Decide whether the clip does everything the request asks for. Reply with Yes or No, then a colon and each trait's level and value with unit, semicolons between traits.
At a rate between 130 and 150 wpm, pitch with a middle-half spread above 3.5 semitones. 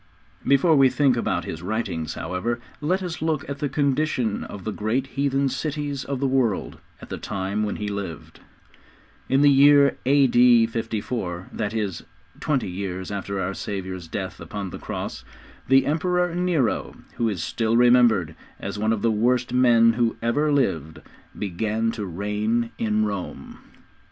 No: average, 160 wpm; average, 5.3 semitones